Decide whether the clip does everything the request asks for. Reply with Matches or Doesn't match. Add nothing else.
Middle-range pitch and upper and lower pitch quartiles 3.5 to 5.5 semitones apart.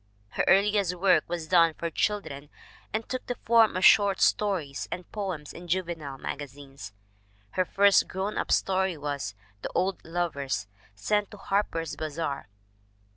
Matches